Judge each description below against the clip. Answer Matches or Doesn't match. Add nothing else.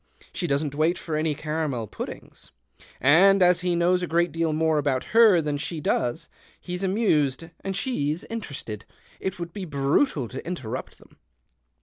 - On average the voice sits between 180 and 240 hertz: Doesn't match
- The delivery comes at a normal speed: Matches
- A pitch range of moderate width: Matches